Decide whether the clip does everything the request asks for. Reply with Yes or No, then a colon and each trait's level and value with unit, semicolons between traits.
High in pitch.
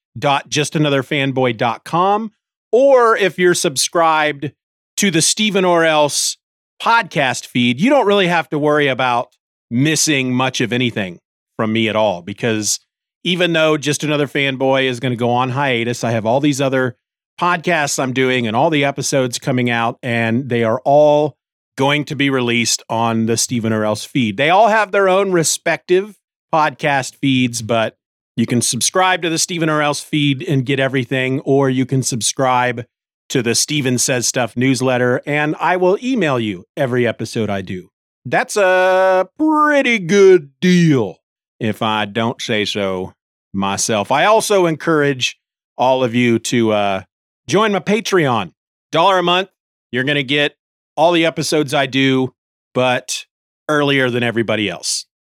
No: low, 135 Hz